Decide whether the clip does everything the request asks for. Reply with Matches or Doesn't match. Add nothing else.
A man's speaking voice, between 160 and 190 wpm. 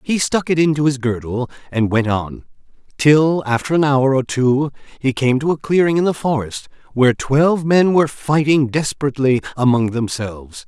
Matches